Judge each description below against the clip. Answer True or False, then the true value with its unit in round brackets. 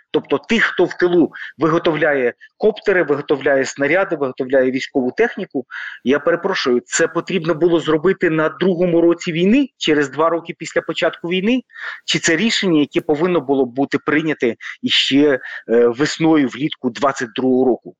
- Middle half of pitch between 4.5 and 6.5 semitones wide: True (4.8 semitones)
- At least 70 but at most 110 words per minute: False (140 wpm)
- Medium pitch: True (165 Hz)